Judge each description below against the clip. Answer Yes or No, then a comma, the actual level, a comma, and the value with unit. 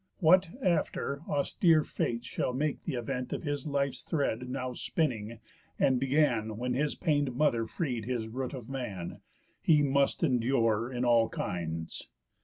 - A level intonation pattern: No, average, 3.7 semitones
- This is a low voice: Yes, low, 130 Hz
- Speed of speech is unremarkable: Yes, average, 150 wpm